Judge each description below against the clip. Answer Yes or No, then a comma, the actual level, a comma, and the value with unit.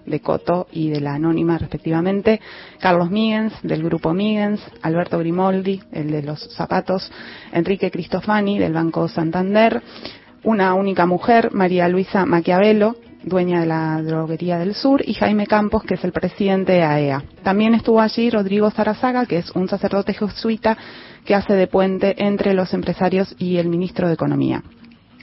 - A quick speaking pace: No, average, 155 wpm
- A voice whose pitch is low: No, medium, 185 Hz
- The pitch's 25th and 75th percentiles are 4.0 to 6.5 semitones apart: No, average, 3.6 semitones